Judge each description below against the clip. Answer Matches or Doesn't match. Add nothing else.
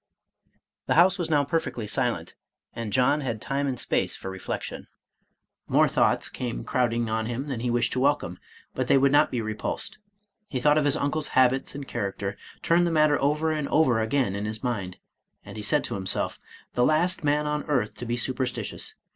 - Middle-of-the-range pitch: Doesn't match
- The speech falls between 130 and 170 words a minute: Doesn't match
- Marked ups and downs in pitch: Doesn't match